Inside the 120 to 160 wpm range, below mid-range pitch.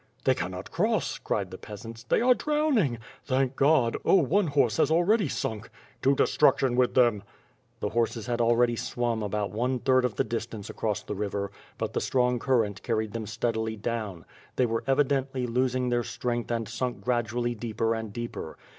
No: average, 180 wpm; low, 120 Hz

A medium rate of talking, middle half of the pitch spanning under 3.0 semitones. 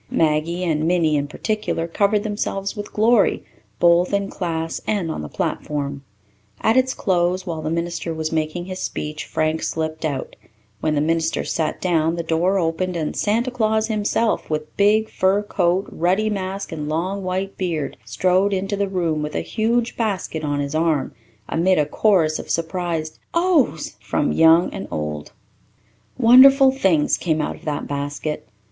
No: average, 165 wpm; average, 4.3 semitones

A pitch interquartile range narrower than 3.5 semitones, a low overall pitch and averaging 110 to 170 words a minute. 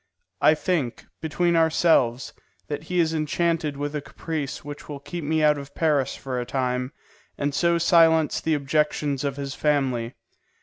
No: average, 2.8 semitones; medium, 150 Hz; average, 165 wpm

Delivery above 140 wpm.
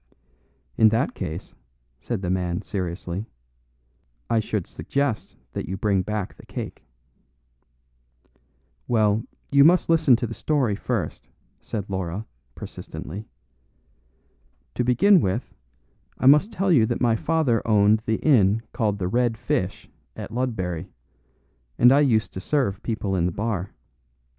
No: slow, 135 wpm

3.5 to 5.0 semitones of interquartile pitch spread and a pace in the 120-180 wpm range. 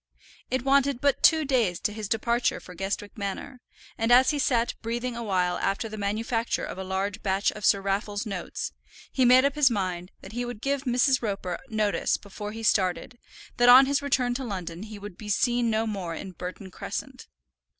No: average, 4.0 semitones; average, 200 wpm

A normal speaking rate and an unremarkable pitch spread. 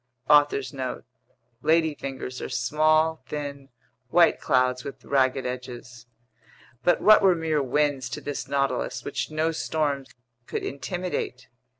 No: slow, 125 wpm; average, 3.4 semitones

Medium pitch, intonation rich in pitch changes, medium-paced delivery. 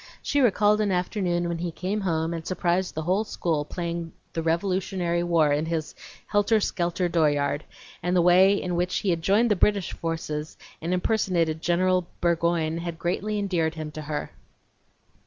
No: medium, 175 Hz; narrow, 2.4 semitones; average, 170 wpm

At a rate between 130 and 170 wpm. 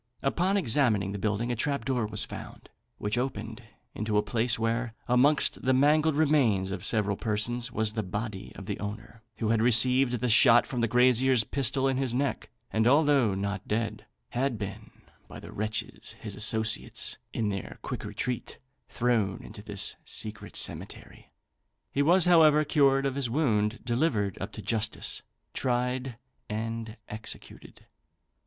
Yes: average, 155 wpm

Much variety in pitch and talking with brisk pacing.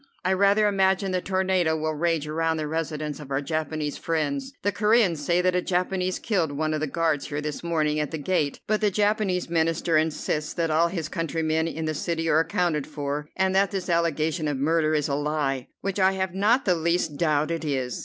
No: average, 3.4 semitones; fast, 215 wpm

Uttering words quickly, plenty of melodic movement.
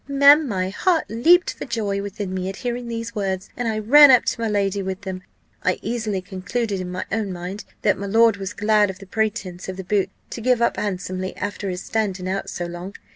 No: fast, 225 wpm; average, 3.3 semitones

